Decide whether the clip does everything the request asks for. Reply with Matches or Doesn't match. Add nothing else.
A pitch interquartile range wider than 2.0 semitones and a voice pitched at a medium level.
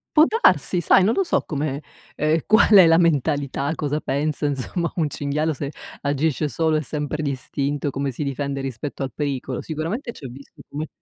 Matches